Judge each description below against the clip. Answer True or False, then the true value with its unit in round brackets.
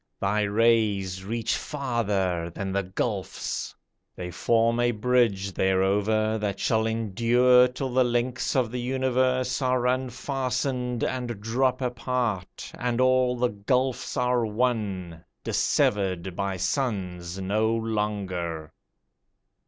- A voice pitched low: True (115 Hz)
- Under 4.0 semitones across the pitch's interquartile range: False (4.3 semitones)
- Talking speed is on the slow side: True (115 wpm)